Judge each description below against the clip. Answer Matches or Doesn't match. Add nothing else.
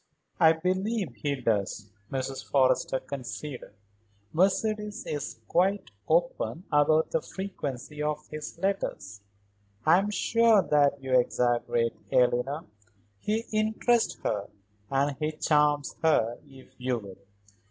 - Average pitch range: Doesn't match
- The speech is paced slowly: Matches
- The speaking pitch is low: Doesn't match